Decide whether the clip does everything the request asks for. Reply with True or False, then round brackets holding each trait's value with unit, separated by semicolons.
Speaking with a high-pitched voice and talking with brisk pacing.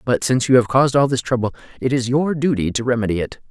False (125 Hz; 255 wpm)